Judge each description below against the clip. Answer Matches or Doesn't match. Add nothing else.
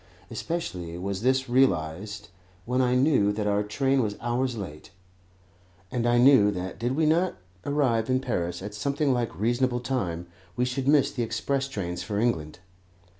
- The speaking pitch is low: Matches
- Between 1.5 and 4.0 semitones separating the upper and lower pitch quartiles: Doesn't match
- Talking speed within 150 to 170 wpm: Matches